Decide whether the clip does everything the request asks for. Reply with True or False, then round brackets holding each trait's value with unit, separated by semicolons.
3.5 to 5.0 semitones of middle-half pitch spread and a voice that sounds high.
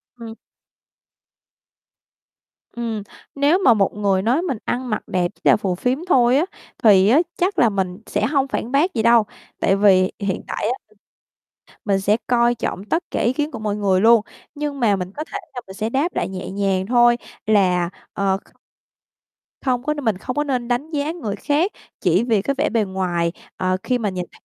False (5.5 semitones; 225 Hz)